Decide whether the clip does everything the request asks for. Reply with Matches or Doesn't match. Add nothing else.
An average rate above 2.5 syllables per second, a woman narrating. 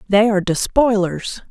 Matches